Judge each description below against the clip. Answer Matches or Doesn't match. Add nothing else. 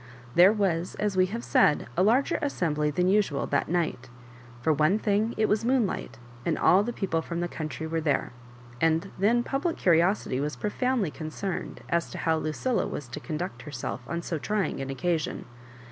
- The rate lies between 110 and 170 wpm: Doesn't match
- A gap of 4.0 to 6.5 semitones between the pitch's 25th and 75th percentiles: Matches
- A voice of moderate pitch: Matches